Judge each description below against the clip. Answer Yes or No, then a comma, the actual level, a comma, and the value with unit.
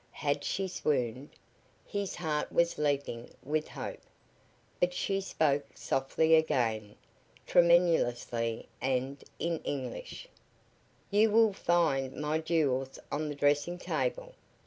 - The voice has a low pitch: No, medium, 150 Hz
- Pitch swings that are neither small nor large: Yes, average, 4.5 semitones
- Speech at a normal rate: No, slow, 110 wpm